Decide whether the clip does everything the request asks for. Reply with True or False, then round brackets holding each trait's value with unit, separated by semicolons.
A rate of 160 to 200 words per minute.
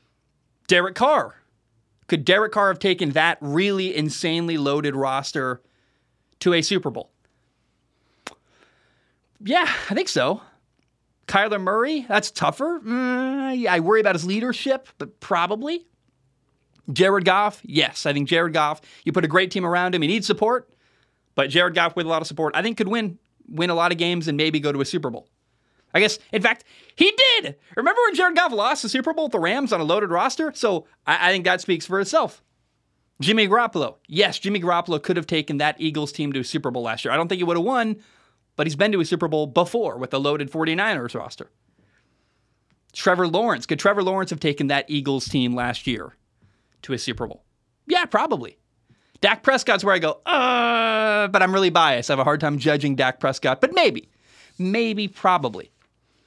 True (190 wpm)